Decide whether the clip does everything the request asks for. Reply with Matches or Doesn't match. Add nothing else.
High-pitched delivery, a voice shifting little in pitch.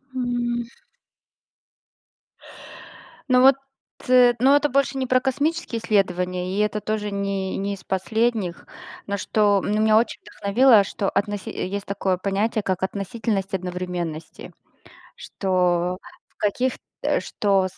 Doesn't match